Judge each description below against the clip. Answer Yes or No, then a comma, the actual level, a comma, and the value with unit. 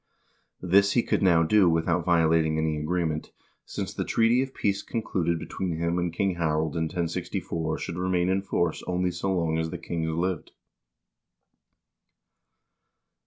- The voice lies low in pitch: Yes, very low, 85 Hz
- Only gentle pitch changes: Yes, narrow, 2.3 semitones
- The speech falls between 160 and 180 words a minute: No, average, 150 wpm